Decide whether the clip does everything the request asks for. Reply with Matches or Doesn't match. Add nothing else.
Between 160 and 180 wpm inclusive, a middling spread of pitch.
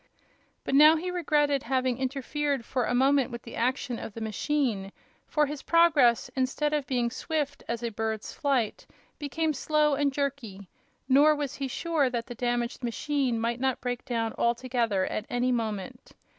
Matches